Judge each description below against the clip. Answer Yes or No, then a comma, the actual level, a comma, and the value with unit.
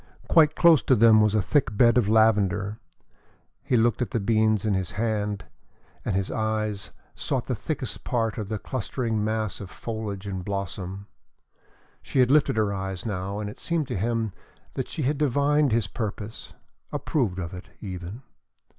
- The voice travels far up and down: No, average, 2.9 semitones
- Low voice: Yes, low, 110 Hz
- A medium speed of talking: Yes, average, 170 wpm